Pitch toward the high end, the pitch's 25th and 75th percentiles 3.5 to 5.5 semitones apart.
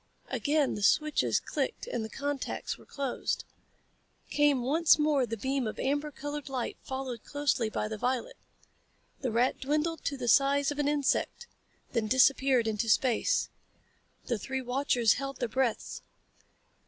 No: very high, 265 Hz; average, 3.1 semitones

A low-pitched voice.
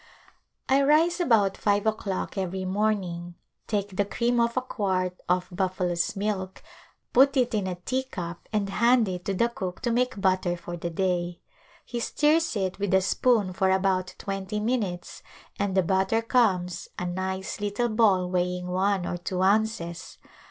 No: high, 195 Hz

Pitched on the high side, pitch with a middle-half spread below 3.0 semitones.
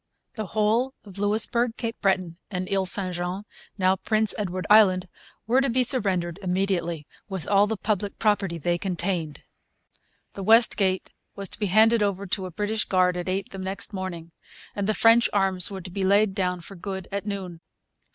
Yes: high, 195 Hz; narrow, 2.4 semitones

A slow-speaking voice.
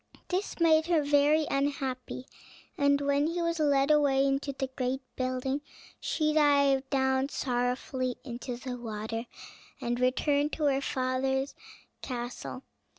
Yes: slow, 130 wpm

